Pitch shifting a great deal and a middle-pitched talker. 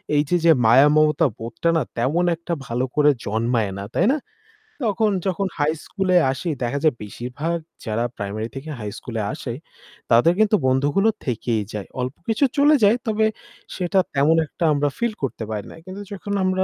Yes: wide, 7.9 semitones; medium, 145 Hz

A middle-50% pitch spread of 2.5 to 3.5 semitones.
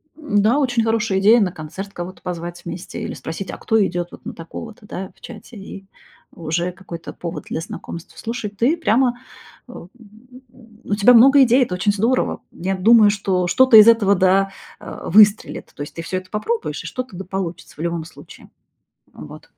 No: average, 4.3 semitones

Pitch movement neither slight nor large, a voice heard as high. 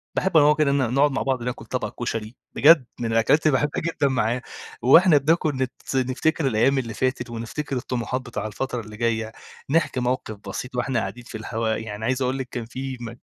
No: average, 3.1 semitones; low, 125 Hz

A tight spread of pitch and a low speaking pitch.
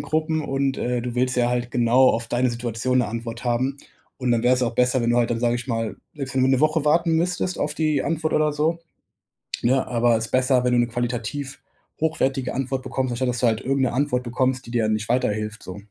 Yes: narrow, 2.3 semitones; low, 125 Hz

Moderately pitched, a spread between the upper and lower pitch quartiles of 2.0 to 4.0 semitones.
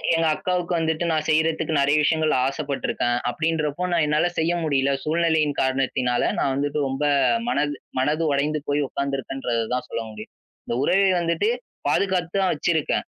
Yes: medium, 155 Hz; average, 2.9 semitones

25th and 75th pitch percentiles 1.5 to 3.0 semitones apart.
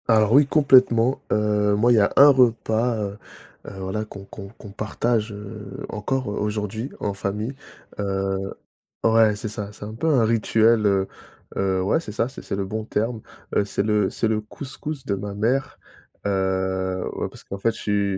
Yes: narrow, 2.5 semitones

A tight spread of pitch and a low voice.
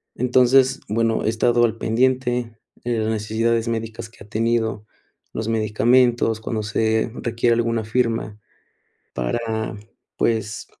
Yes: narrow, 1.3 semitones; low, 115 Hz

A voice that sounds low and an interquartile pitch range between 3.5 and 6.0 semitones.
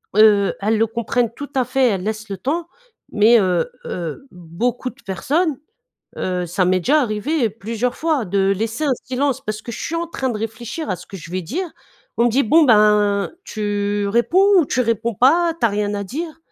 No: high, 225 Hz; average, 4.8 semitones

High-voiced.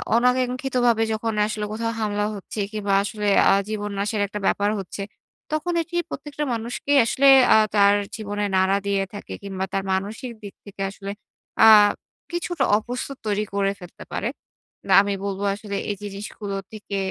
Yes: high, 210 Hz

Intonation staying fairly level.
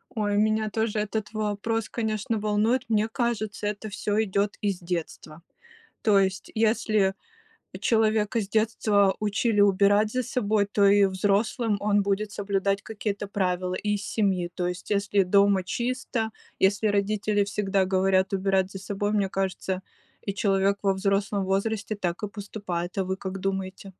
Yes: narrow, 1.8 semitones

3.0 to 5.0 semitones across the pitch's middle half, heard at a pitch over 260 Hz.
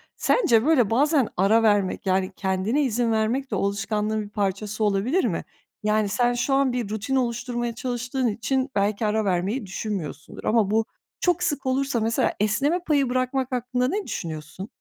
No: average, 4.0 semitones; high, 225 Hz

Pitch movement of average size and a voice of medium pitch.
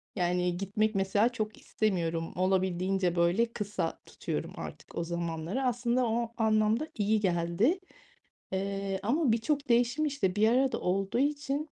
No: average, 4.6 semitones; high, 210 Hz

